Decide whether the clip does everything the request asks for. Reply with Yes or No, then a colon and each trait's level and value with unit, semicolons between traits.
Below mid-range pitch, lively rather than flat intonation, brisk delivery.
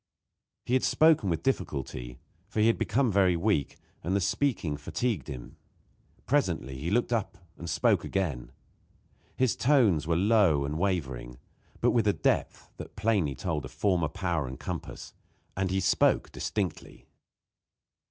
No: very low, 90 Hz; wide, 6.2 semitones; average, 150 wpm